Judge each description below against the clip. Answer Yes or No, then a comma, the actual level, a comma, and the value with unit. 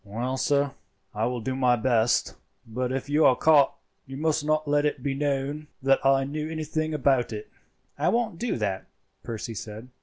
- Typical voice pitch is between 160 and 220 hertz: No, low, 135 Hz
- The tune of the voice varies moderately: Yes, average, 3.5 semitones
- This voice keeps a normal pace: Yes, average, 185 wpm